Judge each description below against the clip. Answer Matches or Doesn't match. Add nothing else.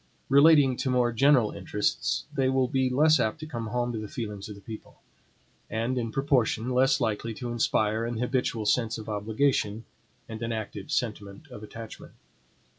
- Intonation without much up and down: Doesn't match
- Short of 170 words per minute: Doesn't match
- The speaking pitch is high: Doesn't match